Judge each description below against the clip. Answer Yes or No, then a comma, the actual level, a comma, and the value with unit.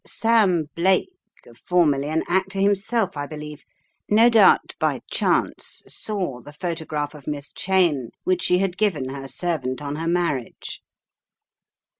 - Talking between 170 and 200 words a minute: No, slow, 135 wpm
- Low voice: No, medium, 170 Hz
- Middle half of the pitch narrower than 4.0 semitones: No, average, 4.9 semitones